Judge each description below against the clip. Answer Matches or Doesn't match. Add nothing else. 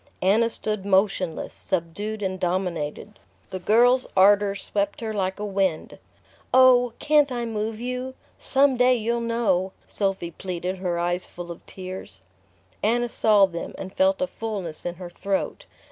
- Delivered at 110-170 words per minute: Matches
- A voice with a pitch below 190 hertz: Doesn't match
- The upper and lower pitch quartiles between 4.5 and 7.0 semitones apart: Doesn't match